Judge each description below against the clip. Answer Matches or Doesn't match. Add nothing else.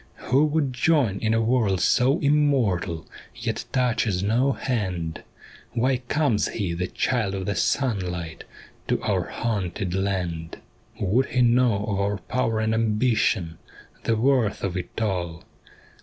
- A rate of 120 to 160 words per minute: Matches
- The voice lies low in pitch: Matches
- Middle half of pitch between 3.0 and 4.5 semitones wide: Doesn't match